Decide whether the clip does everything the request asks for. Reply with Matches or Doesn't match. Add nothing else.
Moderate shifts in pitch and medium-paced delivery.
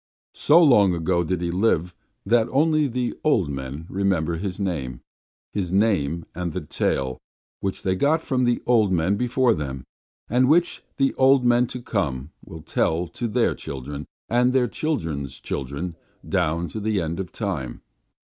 Doesn't match